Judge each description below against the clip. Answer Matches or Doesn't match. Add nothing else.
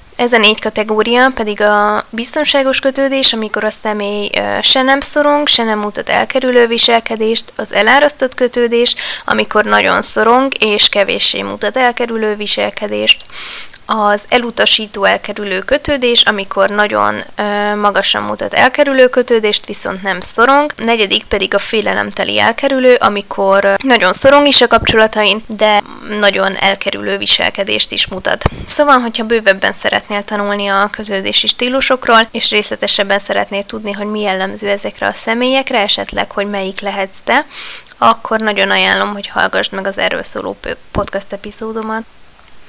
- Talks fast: Doesn't match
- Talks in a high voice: Matches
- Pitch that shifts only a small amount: Doesn't match